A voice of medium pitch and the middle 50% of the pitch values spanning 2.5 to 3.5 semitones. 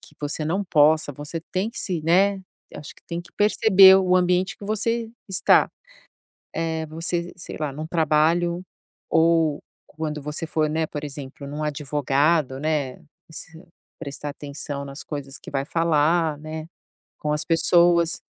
Yes: medium, 160 Hz; average, 2.8 semitones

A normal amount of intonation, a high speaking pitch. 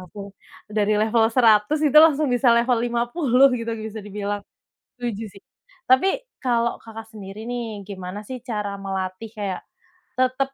Yes: average, 3.1 semitones; high, 225 Hz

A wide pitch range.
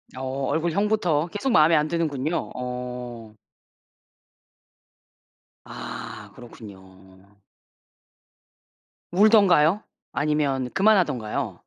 Yes: wide, 6.1 semitones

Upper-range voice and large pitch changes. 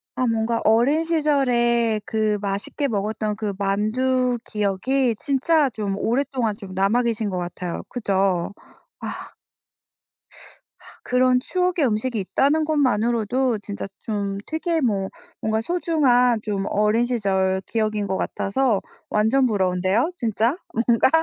No: high, 225 Hz; average, 4.1 semitones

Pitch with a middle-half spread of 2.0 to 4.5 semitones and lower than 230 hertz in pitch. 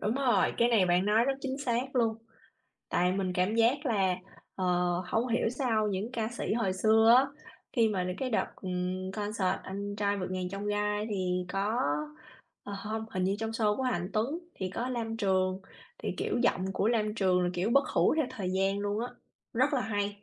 Yes: average, 3.6 semitones; high, 210 Hz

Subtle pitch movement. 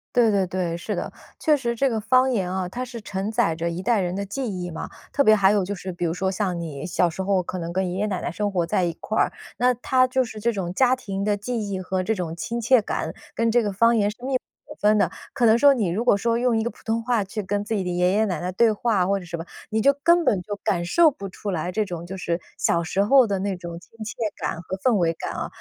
No: average, 4.3 semitones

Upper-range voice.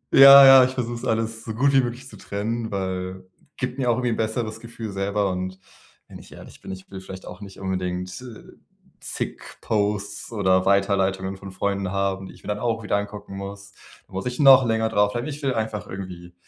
No: low, 105 Hz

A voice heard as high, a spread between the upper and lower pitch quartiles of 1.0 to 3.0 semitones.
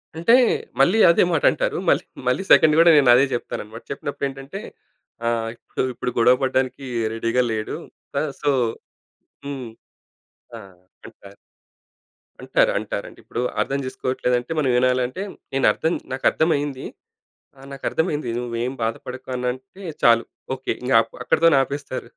No: low, 130 Hz; average, 2.7 semitones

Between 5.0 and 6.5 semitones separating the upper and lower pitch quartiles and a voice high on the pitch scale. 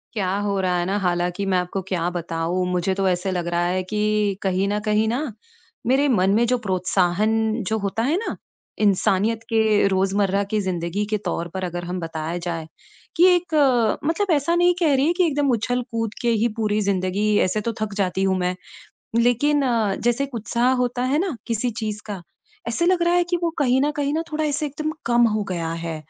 Yes: average, 5.3 semitones; high, 210 Hz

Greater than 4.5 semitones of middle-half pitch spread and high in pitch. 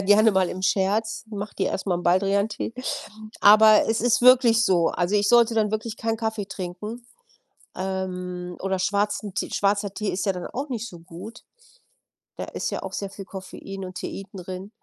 No: average, 2.7 semitones; high, 200 Hz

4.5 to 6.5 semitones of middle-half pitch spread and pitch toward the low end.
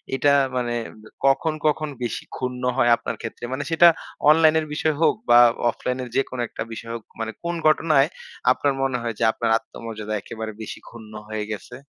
Yes: average, 4.8 semitones; low, 125 Hz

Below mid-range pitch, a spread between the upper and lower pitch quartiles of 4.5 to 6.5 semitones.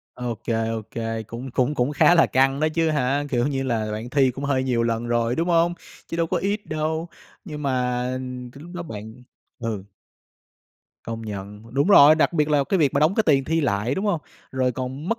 Yes: low, 130 Hz; average, 4.8 semitones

